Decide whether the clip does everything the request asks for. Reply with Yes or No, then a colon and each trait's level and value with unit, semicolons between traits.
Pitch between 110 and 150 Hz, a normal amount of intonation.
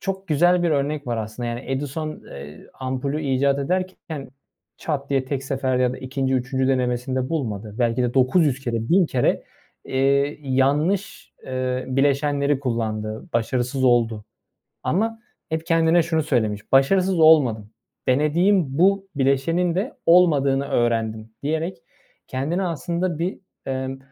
Yes: low, 135 Hz; average, 4.2 semitones